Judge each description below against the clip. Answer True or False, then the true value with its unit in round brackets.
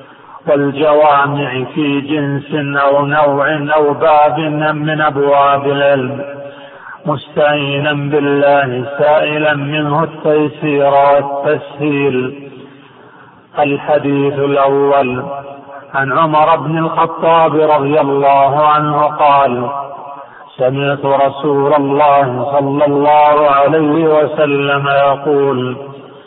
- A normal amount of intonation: False (1.3 semitones)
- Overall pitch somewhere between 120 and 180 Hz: True (140 Hz)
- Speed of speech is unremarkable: True (80 wpm)